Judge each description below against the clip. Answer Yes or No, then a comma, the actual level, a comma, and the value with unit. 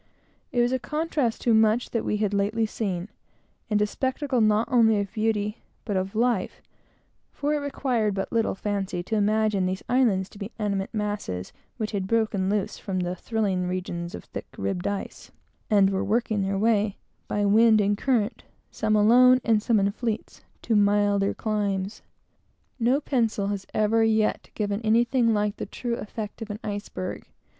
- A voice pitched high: Yes, high, 210 Hz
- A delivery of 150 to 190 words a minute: Yes, average, 170 wpm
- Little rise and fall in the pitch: Yes, narrow, 2.3 semitones